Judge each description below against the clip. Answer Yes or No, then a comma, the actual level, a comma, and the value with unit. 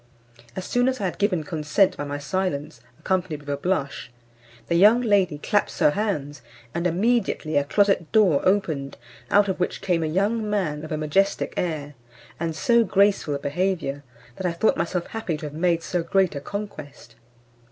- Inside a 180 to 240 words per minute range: Yes, average, 185 wpm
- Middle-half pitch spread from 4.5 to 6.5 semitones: Yes, average, 4.9 semitones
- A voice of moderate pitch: Yes, medium, 175 Hz